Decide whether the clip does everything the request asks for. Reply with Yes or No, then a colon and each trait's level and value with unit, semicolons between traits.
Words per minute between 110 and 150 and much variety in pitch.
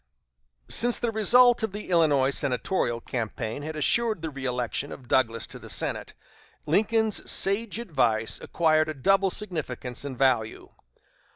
Yes: slow, 135 wpm; wide, 8.4 semitones